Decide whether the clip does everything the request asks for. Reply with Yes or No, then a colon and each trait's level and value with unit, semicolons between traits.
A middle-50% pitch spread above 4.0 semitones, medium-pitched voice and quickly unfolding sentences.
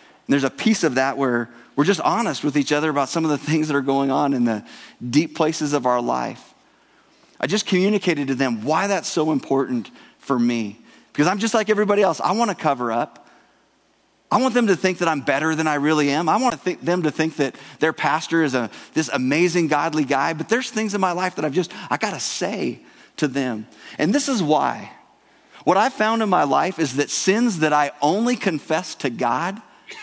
Yes: average, 5.0 semitones; medium, 155 Hz; fast, 225 wpm